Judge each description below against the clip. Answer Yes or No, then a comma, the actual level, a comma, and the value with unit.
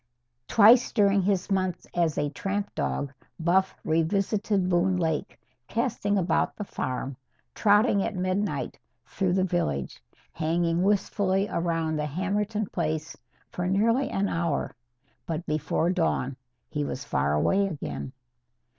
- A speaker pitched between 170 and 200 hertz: Yes, medium, 185 Hz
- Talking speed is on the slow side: Yes, slow, 130 wpm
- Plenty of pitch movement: No, average, 3.9 semitones